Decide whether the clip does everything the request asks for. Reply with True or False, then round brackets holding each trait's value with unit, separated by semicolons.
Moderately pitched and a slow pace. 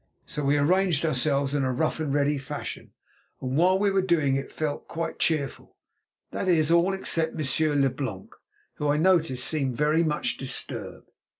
False (150 Hz; 165 wpm)